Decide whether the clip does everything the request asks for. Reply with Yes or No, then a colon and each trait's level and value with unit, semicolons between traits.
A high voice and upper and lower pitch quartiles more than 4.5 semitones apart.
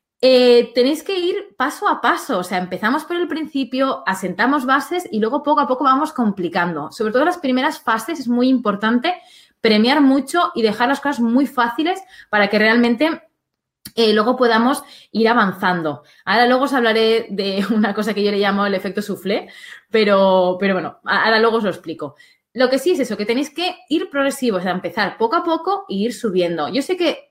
Yes: high, 240 Hz; wide, 5.6 semitones